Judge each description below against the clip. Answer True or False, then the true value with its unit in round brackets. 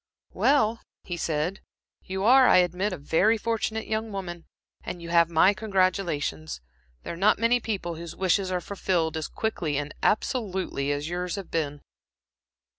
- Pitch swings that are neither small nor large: True (4.3 semitones)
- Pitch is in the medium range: True (180 Hz)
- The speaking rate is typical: True (160 wpm)